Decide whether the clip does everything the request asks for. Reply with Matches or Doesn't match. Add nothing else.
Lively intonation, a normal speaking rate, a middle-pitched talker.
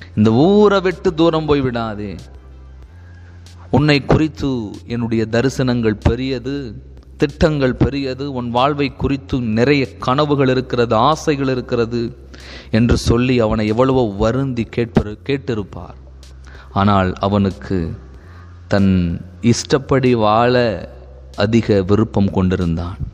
Doesn't match